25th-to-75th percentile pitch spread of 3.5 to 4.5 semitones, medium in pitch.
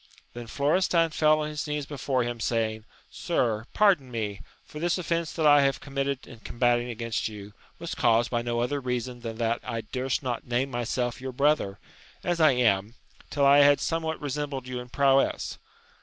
No: average, 3.8 semitones; low, 130 Hz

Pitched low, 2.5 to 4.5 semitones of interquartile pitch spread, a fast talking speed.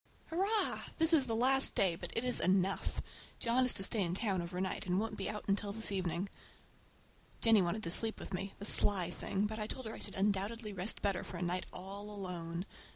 No: high, 200 Hz; average, 3.4 semitones; fast, 220 wpm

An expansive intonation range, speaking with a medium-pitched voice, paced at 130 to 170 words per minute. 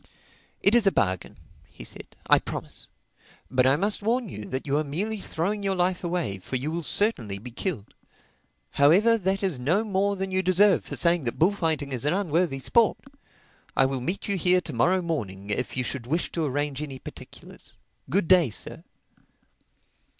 No: wide, 6.5 semitones; medium, 170 Hz; average, 180 wpm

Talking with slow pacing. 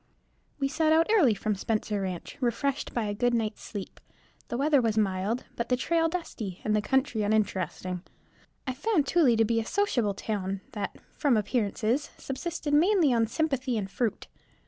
No: average, 175 wpm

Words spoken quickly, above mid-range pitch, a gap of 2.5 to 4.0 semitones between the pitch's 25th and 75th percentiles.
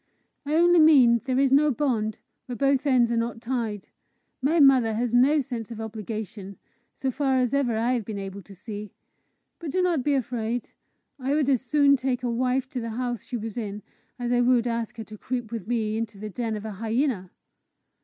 Yes: fast, 210 wpm; high, 240 Hz; average, 3.2 semitones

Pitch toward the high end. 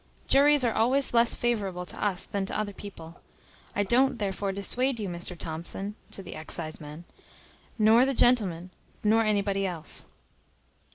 Yes: high, 200 Hz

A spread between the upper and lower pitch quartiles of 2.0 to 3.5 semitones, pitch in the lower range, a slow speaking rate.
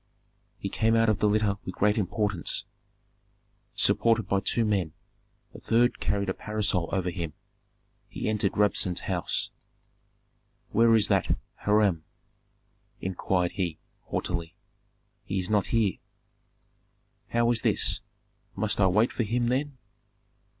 Yes: average, 3.2 semitones; low, 105 Hz; slow, 130 wpm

